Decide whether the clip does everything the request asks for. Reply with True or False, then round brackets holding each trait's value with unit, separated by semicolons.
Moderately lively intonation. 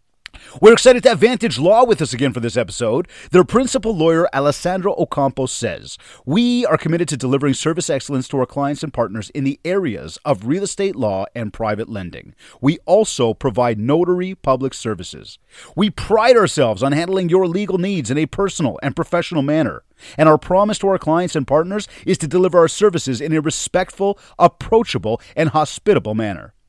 False (6.2 semitones)